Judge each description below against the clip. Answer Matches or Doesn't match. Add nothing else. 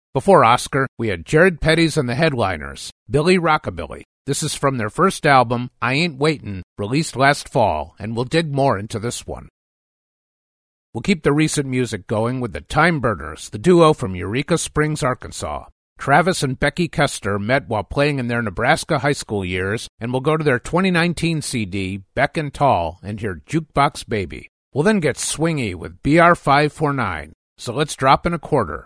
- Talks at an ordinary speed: Matches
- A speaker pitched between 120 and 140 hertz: Matches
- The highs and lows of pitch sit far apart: Matches